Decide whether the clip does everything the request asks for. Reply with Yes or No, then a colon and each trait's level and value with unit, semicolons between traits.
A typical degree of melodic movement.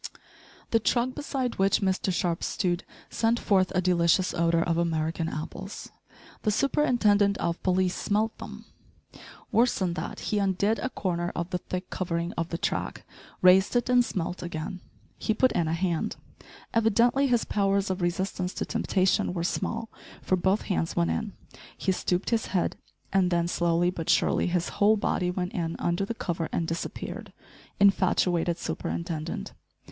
Yes: average, 3.2 semitones